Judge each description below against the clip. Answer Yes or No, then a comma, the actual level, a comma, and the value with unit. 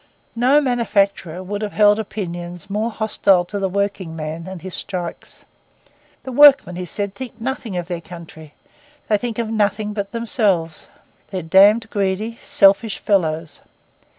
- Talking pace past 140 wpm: Yes, average, 150 wpm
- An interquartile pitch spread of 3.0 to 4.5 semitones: Yes, average, 3.8 semitones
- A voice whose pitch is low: No, high, 200 Hz